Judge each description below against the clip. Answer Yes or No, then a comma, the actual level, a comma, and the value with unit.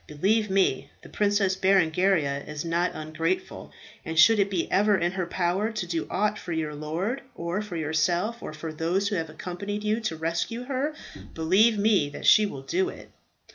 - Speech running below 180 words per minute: No, average, 185 wpm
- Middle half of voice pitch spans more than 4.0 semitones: Yes, average, 4.4 semitones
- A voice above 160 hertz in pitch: Yes, medium, 185 Hz